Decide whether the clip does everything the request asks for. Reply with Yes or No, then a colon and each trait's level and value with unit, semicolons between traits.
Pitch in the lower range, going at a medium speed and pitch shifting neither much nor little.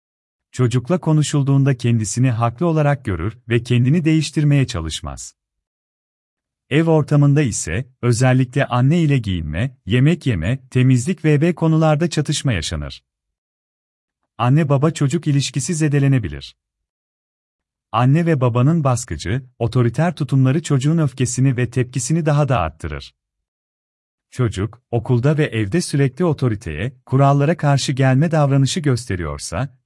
No: low, 130 Hz; average, 105 wpm; wide, 7.1 semitones